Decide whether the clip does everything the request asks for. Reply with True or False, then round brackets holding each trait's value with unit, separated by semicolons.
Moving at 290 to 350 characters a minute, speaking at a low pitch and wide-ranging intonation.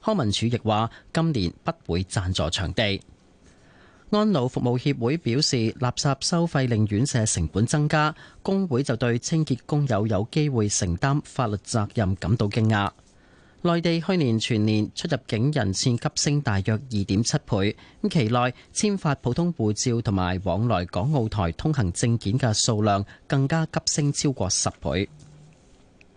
False (235 characters per minute; 120 Hz; 6.3 semitones)